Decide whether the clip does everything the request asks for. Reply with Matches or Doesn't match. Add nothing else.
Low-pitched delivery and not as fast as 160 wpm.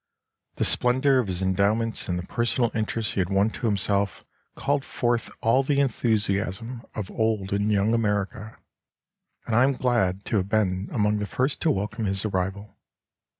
Doesn't match